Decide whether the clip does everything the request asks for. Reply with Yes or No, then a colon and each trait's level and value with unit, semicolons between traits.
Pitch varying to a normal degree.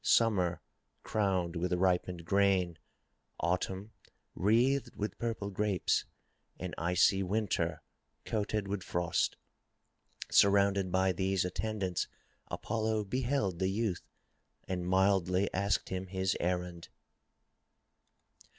No: narrow, 2.3 semitones